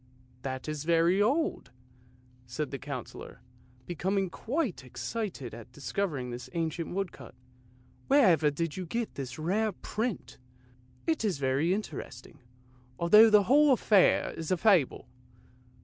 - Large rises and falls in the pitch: Yes, wide, 7.2 semitones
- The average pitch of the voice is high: No, medium, 170 Hz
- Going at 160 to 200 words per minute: No, slow, 135 wpm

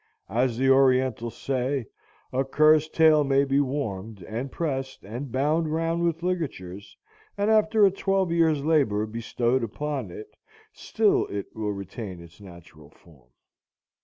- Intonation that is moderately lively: No, wide, 6.5 semitones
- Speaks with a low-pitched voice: Yes, low, 130 Hz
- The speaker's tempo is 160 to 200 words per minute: No, average, 140 wpm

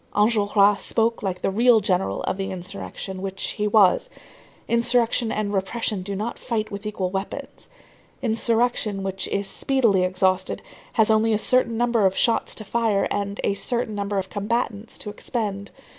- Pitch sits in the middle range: No, high, 205 Hz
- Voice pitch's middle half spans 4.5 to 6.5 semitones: No, average, 2.8 semitones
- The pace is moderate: Yes, average, 160 wpm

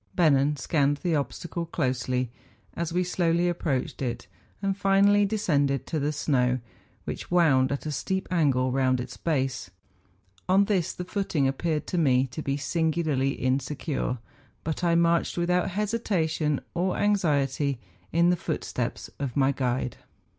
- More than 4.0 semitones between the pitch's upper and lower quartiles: Yes, average, 4.7 semitones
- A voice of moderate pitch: Yes, medium, 155 Hz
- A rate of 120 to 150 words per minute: Yes, average, 145 wpm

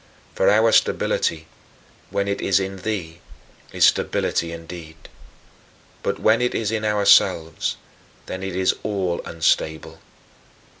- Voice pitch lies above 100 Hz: No, very low, 95 Hz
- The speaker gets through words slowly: Yes, slow, 120 wpm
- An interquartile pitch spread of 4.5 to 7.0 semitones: No, average, 4.1 semitones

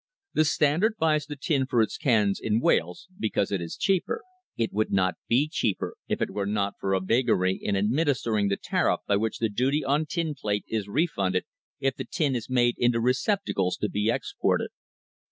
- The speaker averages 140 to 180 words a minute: No, average, 195 wpm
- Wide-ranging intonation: Yes, wide, 6.1 semitones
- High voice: No, low, 115 Hz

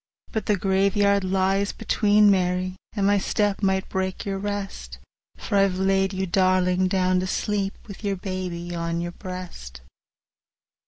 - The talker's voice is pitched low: No, high, 190 Hz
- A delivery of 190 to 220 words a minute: No, average, 155 wpm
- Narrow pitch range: Yes, narrow, 1.5 semitones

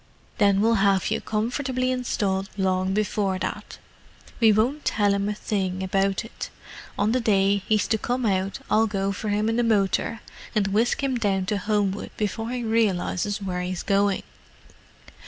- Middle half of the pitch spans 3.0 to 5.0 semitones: No, narrow, 2.5 semitones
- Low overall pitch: No, high, 205 Hz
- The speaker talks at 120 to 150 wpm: No, average, 170 wpm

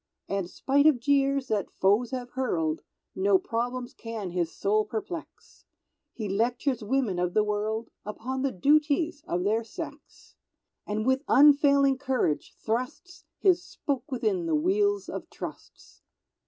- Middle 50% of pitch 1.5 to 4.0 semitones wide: No, average, 5.2 semitones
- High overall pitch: Yes, very high, 250 Hz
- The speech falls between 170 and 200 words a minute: No, average, 140 wpm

